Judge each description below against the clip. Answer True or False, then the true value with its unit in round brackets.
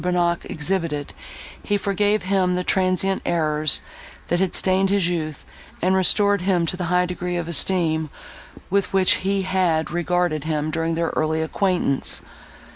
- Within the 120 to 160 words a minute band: True (150 wpm)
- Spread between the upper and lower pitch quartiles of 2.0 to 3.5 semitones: True (2.7 semitones)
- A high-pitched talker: False (180 Hz)